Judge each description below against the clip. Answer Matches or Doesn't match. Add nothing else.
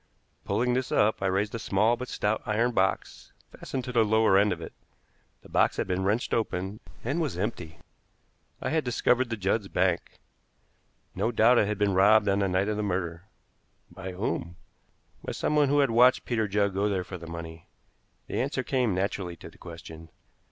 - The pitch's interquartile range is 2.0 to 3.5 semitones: Doesn't match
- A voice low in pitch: Matches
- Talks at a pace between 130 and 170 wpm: Doesn't match